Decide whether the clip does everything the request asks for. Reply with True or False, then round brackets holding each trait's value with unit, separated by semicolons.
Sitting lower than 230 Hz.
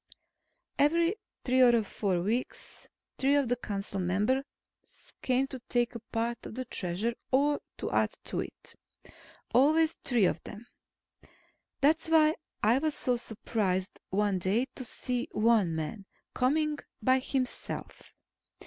False (240 Hz)